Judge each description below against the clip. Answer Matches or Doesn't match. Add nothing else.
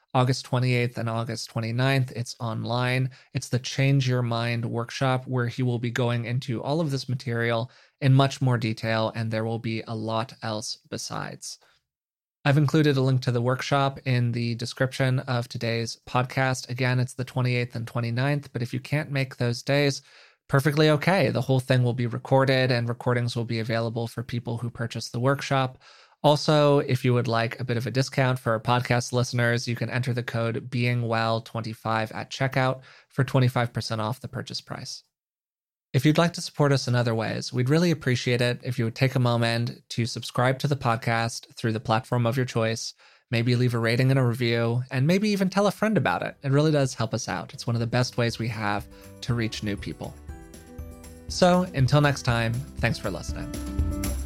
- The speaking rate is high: Doesn't match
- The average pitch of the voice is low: Matches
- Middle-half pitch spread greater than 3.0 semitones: Doesn't match